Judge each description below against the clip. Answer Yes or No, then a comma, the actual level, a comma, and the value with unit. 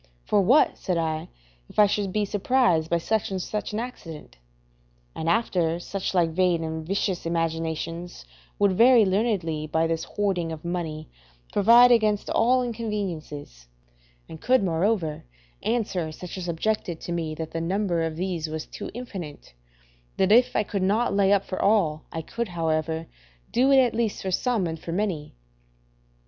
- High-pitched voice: No, medium, 180 Hz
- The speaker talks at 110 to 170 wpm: Yes, average, 165 wpm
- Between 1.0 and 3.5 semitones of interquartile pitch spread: No, average, 4.5 semitones